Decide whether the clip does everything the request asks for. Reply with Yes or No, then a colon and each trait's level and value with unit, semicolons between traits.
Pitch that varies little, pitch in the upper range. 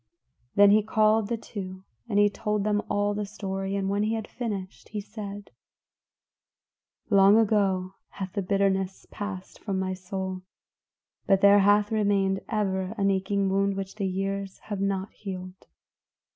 Yes: narrow, 1.3 semitones; high, 200 Hz